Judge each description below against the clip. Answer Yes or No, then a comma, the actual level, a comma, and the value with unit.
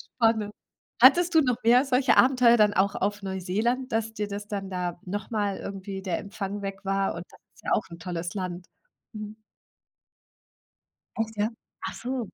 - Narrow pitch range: No, average, 3.2 semitones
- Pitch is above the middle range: Yes, high, 205 Hz